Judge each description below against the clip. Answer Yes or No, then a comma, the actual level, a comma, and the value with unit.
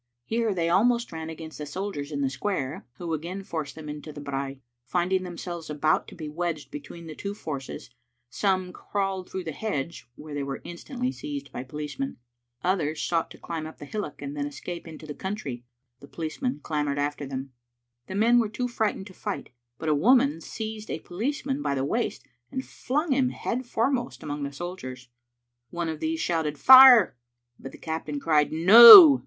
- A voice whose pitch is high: No, medium, 170 Hz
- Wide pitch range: Yes, wide, 6.7 semitones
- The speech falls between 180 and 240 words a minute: Yes, average, 195 wpm